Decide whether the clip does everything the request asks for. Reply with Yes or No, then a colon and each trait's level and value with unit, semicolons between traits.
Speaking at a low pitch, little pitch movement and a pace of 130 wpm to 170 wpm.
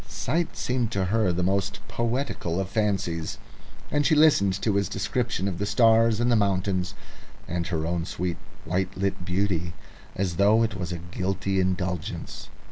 No: very low, 95 Hz; average, 3.5 semitones; average, 165 wpm